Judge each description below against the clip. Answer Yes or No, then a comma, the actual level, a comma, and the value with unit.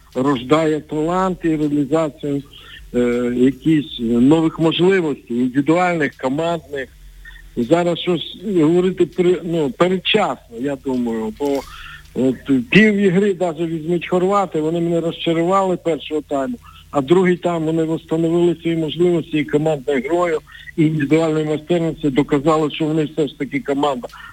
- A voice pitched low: No, medium, 155 Hz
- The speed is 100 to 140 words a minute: Yes, average, 120 wpm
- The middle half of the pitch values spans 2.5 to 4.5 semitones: Yes, average, 3.3 semitones